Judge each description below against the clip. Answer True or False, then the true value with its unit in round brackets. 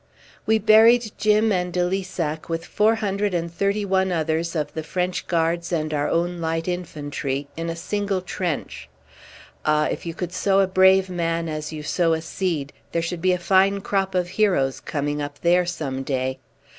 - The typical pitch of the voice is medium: True (175 Hz)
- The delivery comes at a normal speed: True (185 wpm)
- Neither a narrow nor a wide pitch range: True (3.3 semitones)